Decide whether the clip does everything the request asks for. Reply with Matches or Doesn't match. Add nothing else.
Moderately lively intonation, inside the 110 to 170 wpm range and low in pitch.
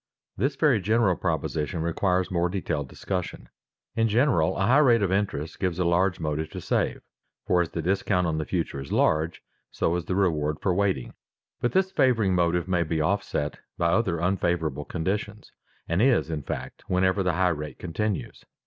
Doesn't match